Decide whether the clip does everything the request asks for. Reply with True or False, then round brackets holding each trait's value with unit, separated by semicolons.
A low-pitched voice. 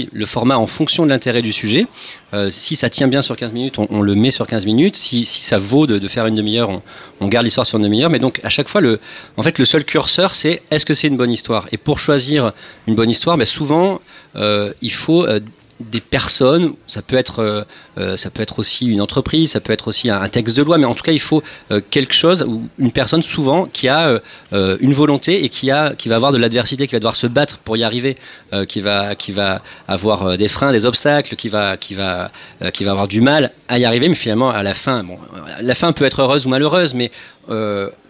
True (120 Hz)